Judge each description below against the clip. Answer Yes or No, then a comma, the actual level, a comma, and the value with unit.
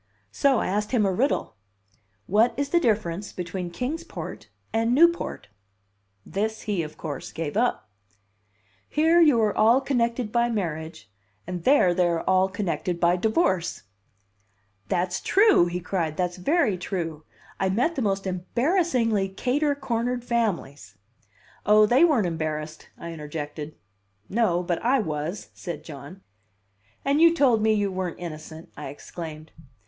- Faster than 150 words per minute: No, average, 145 wpm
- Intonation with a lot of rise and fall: Yes, wide, 6.2 semitones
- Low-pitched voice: No, high, 195 Hz